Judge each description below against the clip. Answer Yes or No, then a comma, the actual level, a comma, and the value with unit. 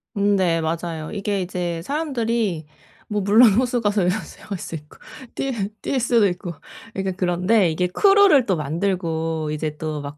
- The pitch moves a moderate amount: Yes, average, 5.0 semitones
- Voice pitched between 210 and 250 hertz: No, medium, 185 Hz